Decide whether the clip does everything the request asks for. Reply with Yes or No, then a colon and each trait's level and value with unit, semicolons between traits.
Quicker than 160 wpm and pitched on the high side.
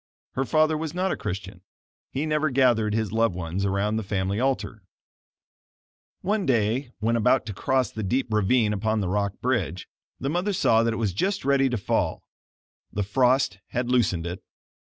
No: average, 175 wpm; low, 115 Hz